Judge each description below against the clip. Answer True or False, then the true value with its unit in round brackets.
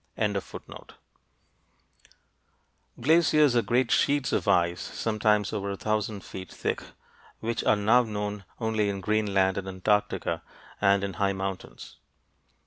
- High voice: False (105 Hz)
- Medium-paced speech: False (120 wpm)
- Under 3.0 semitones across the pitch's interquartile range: True (2.4 semitones)